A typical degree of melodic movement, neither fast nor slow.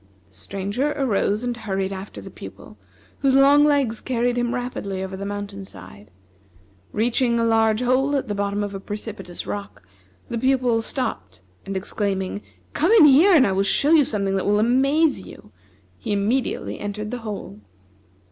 Yes: average, 4.6 semitones; average, 170 wpm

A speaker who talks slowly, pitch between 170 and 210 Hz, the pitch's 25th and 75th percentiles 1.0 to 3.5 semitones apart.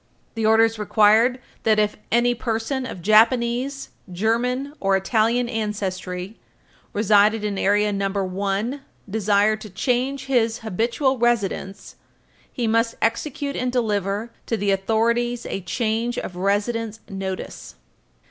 No: slow, 120 wpm; high, 220 Hz; average, 3.0 semitones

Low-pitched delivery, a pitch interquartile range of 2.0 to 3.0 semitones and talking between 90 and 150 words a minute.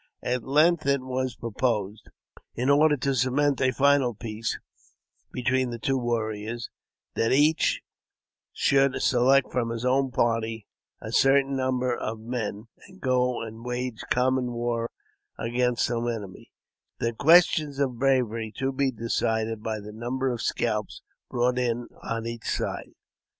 Yes: low, 125 Hz; narrow, 2.5 semitones; average, 145 wpm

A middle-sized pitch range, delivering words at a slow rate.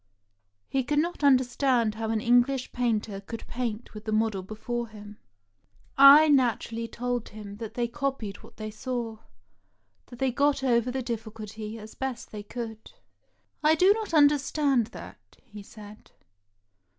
No: average, 3.6 semitones; average, 150 wpm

